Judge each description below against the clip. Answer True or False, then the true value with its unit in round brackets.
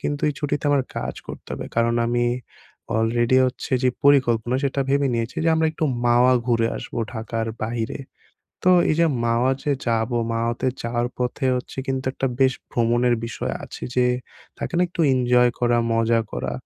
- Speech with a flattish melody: True (2.3 semitones)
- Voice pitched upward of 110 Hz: True (120 Hz)